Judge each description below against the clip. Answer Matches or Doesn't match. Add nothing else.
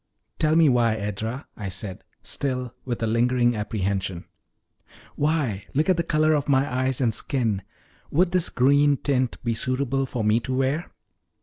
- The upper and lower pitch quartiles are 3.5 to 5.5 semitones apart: Matches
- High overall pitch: Doesn't match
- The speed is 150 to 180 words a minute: Matches